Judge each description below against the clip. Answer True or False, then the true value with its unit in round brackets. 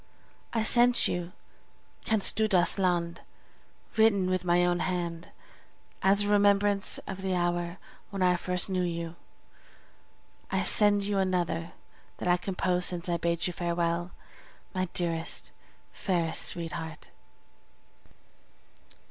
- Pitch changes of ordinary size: False (2.2 semitones)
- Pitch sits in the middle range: True (180 Hz)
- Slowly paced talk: True (125 wpm)